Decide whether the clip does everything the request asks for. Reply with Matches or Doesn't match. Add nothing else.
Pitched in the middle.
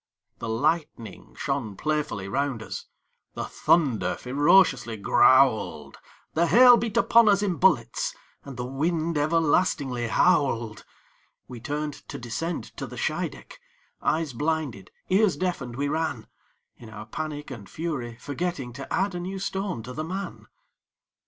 Matches